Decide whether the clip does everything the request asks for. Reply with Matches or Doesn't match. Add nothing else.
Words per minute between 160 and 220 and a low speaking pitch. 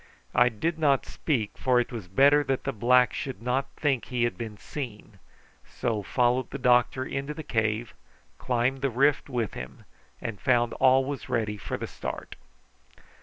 Matches